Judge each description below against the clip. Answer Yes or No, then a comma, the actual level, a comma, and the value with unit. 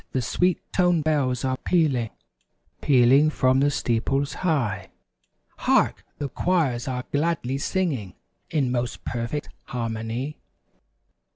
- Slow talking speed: Yes, slow, 110 wpm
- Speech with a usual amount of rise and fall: Yes, average, 4.1 semitones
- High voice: No, low, 135 Hz